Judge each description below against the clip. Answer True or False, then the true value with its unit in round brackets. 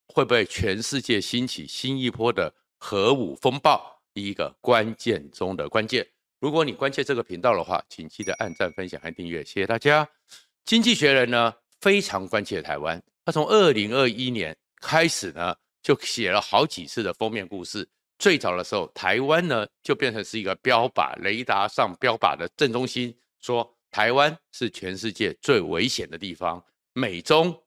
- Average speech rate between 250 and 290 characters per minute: True (260 characters per minute)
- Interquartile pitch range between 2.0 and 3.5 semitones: False (4.5 semitones)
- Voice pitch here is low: True (125 Hz)